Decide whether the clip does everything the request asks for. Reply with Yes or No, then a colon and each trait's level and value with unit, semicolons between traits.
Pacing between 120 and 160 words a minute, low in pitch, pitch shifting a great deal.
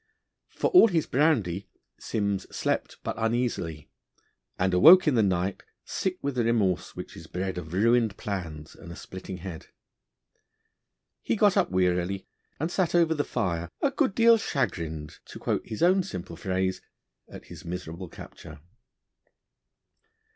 Yes: average, 145 wpm; very low, 95 Hz; wide, 8.0 semitones